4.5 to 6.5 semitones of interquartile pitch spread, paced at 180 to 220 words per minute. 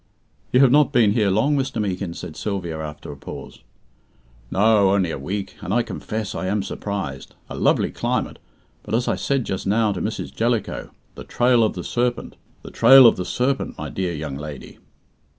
Yes: average, 4.9 semitones; average, 190 wpm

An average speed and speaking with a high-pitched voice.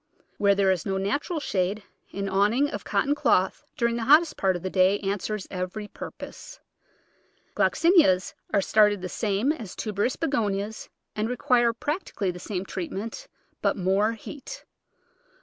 Yes: average, 150 wpm; high, 205 Hz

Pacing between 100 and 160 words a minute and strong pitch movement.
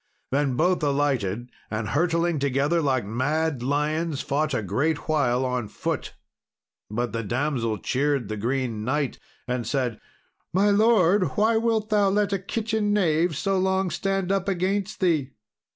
Yes: average, 150 wpm; wide, 6.9 semitones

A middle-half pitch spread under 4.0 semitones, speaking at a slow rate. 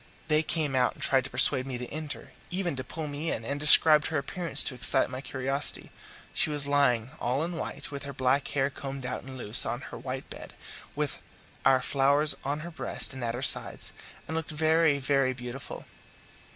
No: narrow, 2.6 semitones; fast, 205 wpm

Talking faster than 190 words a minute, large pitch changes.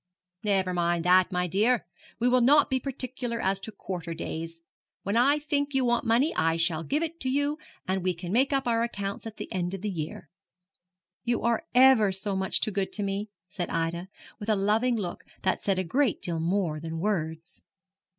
Yes: fast, 205 wpm; wide, 5.7 semitones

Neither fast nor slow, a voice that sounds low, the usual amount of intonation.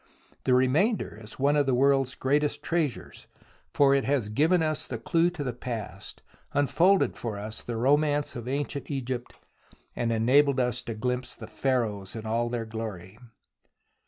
Yes: average, 160 wpm; low, 130 Hz; average, 4.0 semitones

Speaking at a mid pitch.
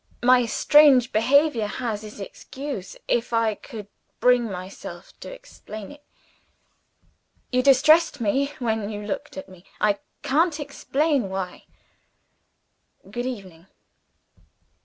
No: high, 240 Hz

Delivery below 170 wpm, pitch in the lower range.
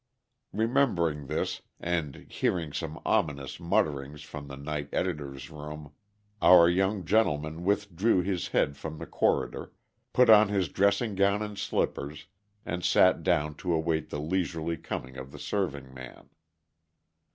Yes: average, 140 wpm; very low, 80 Hz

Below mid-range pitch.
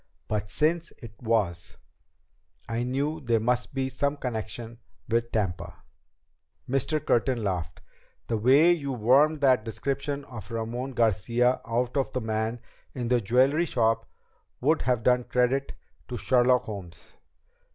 Yes: low, 125 Hz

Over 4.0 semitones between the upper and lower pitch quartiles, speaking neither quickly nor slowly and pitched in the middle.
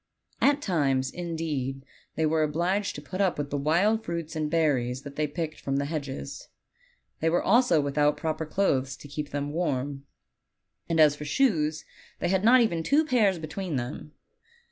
No: average, 3.7 semitones; average, 180 wpm; medium, 155 Hz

